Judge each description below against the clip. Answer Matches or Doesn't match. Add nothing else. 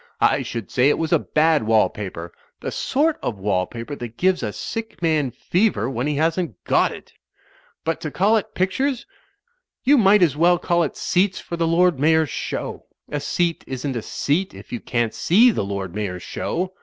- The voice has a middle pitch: Matches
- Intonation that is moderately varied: Doesn't match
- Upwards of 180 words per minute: Matches